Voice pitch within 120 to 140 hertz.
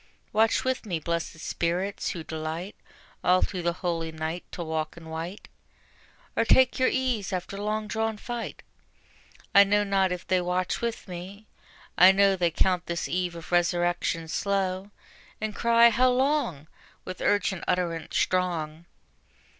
No: medium, 185 Hz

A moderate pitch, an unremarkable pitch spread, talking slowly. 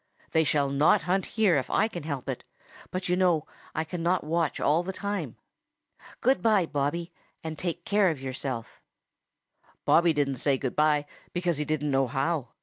No: medium, 160 Hz; average, 3.8 semitones; average, 175 wpm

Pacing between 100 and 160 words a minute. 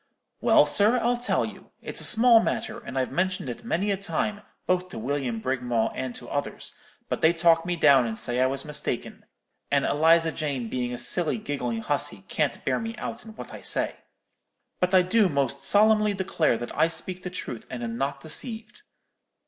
No: average, 195 wpm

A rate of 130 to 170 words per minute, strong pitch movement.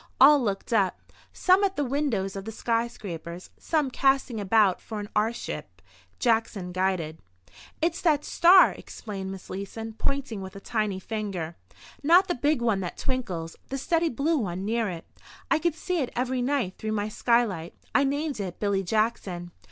Yes: average, 160 wpm; wide, 6.2 semitones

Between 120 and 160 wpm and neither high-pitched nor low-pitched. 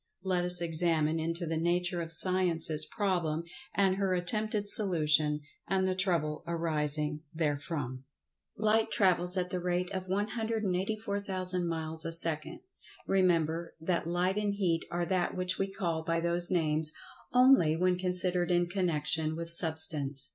Yes: average, 140 wpm; medium, 175 Hz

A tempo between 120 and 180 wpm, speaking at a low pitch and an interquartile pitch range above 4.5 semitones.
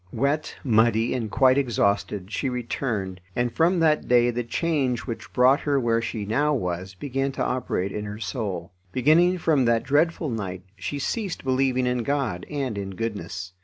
Yes: average, 170 wpm; low, 120 Hz; average, 5.1 semitones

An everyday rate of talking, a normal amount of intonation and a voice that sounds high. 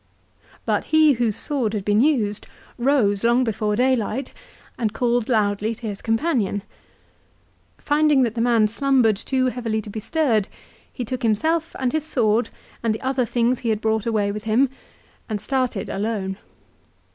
Yes: average, 160 wpm; average, 3.5 semitones; high, 230 Hz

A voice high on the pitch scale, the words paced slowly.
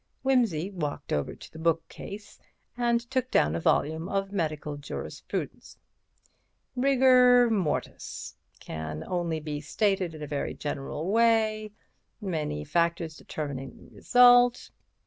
No: medium, 175 Hz; slow, 110 wpm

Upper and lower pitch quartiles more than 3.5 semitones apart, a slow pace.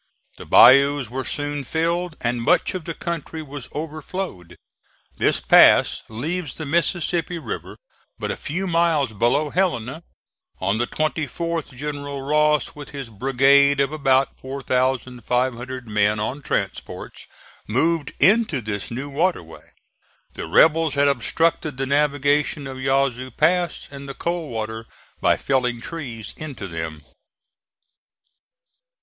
Yes: average, 4.1 semitones; slow, 125 wpm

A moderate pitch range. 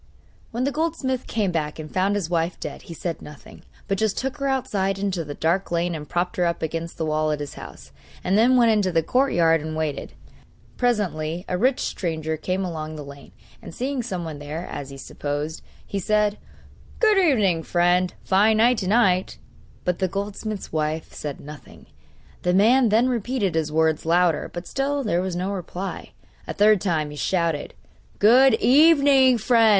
No: wide, 5.9 semitones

